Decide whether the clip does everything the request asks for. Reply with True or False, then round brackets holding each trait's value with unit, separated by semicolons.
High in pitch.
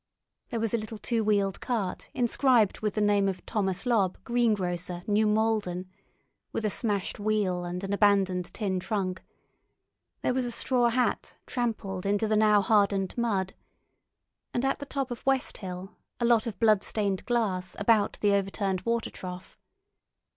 True (210 Hz)